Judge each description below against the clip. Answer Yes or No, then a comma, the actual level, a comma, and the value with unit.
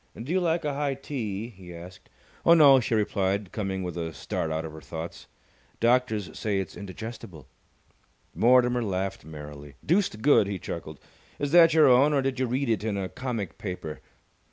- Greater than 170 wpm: Yes, average, 180 wpm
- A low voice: Yes, low, 105 Hz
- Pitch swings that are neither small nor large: No, wide, 6.4 semitones